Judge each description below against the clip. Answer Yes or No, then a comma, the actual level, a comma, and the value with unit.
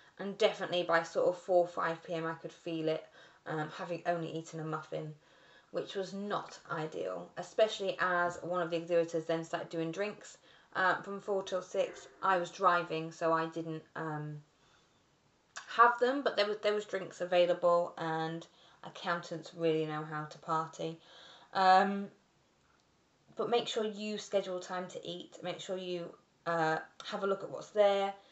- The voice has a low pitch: No, medium, 175 Hz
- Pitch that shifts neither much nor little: Yes, average, 3.0 semitones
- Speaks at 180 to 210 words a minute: No, average, 165 wpm